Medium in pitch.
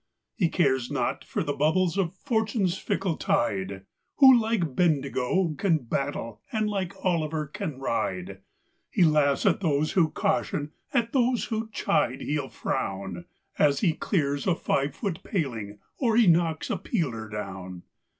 Yes: medium, 155 Hz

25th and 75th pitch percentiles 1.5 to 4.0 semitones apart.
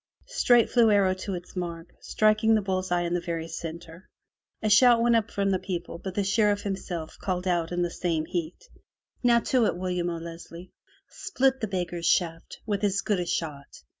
Yes: average, 3.6 semitones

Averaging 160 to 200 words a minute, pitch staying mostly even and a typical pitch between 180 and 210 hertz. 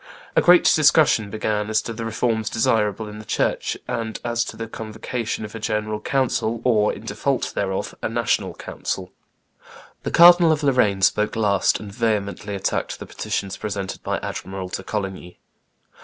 No: average, 165 wpm; narrow, 2.2 semitones; low, 110 Hz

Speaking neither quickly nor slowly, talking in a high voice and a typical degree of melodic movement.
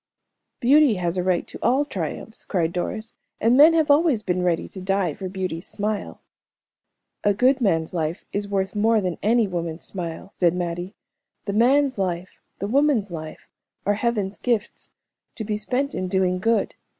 Yes: average, 170 wpm; high, 200 Hz; average, 4.5 semitones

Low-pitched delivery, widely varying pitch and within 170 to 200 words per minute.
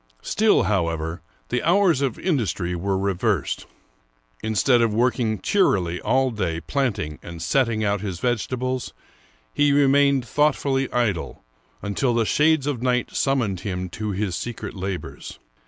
No: low, 115 Hz; wide, 5.9 semitones; slow, 135 wpm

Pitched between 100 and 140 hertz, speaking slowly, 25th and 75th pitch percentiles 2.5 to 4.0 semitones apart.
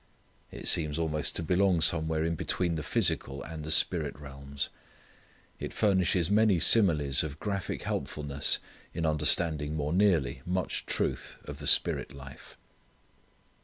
No: very low, 80 Hz; slow, 130 wpm; average, 3.4 semitones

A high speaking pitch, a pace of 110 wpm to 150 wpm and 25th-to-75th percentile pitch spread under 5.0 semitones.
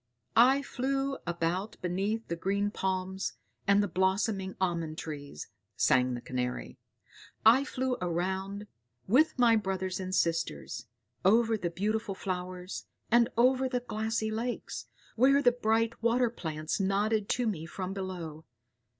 Yes: high, 195 Hz; slow, 135 wpm; average, 4.2 semitones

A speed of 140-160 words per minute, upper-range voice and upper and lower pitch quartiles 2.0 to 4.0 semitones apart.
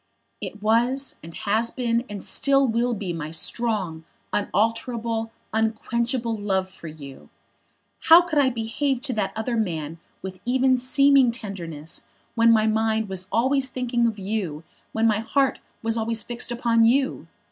Yes: average, 150 wpm; high, 225 Hz; average, 3.3 semitones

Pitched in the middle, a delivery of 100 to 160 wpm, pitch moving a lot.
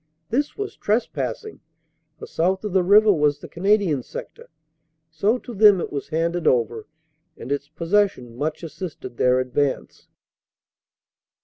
Yes: medium, 170 Hz; average, 140 wpm; wide, 6.3 semitones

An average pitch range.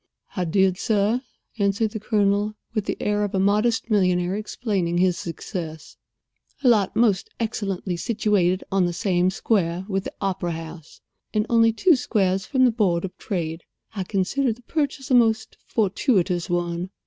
Yes: average, 3.5 semitones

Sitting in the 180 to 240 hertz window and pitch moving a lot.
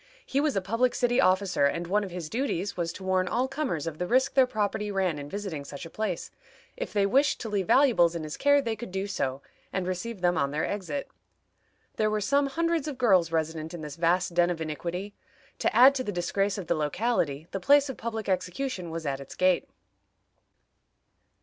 Yes: high, 190 Hz; wide, 6.0 semitones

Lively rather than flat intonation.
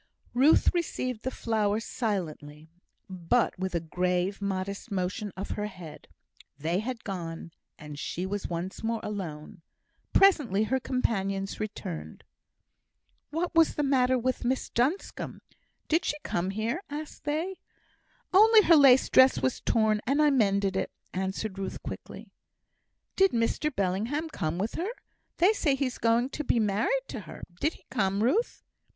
Yes: wide, 6.2 semitones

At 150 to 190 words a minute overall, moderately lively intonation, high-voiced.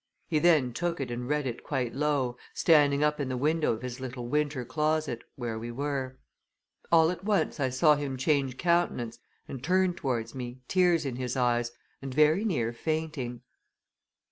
No: average, 175 wpm; average, 4.0 semitones; medium, 140 Hz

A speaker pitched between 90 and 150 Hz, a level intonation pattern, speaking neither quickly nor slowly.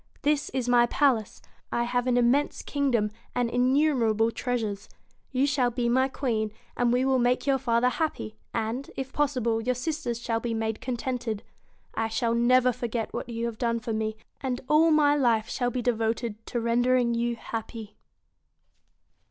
No: high, 240 Hz; narrow, 2.1 semitones; average, 170 wpm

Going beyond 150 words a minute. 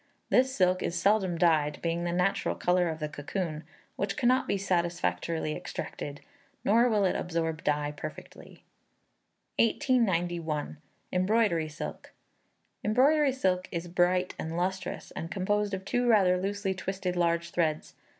No: slow, 135 wpm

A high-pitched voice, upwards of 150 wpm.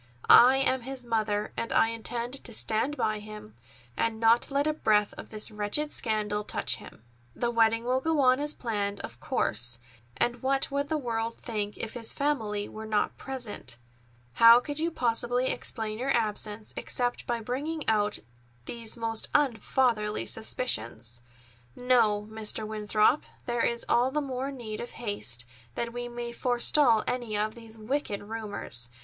Yes: high, 230 Hz; average, 160 wpm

